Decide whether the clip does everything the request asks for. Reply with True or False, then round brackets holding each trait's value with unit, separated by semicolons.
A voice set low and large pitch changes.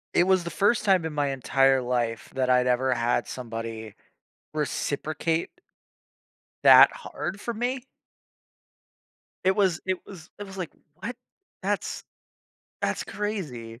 False (150 Hz; 7.2 semitones)